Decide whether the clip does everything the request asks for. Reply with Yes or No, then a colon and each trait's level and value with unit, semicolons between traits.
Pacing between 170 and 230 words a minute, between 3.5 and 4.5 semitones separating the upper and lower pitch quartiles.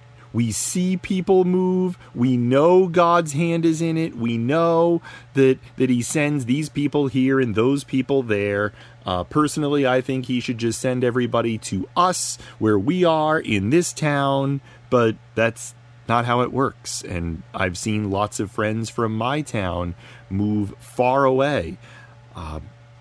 No: average, 155 wpm; average, 4.1 semitones